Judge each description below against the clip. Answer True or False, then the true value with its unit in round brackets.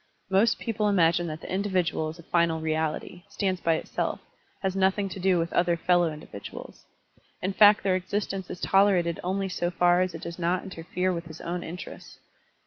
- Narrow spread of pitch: True (2.2 semitones)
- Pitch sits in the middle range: True (180 Hz)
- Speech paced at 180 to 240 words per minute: True (185 wpm)